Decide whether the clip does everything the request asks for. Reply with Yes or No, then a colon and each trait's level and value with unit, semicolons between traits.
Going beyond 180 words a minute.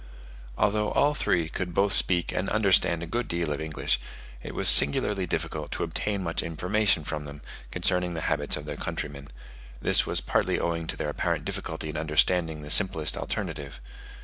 No: average, 175 wpm